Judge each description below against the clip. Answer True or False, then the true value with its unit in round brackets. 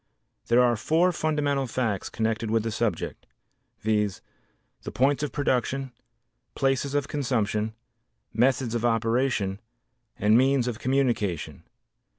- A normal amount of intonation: True (3.7 semitones)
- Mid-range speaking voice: False (120 Hz)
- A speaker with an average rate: False (120 wpm)